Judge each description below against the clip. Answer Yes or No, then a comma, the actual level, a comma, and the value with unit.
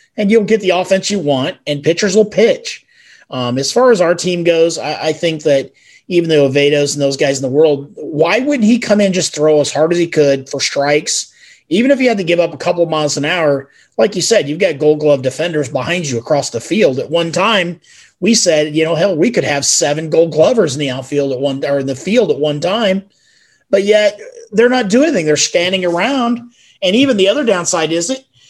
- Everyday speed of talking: No, fast, 240 wpm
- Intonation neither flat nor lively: No, wide, 6.2 semitones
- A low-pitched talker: No, medium, 170 Hz